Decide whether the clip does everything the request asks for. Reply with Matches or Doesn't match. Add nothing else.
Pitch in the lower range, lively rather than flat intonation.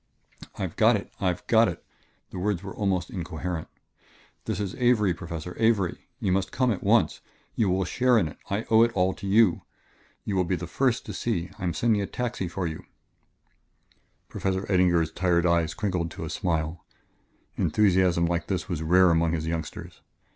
Doesn't match